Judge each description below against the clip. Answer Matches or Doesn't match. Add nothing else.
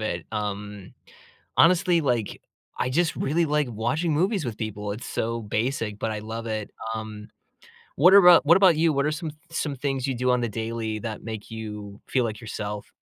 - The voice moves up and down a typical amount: Doesn't match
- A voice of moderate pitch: Doesn't match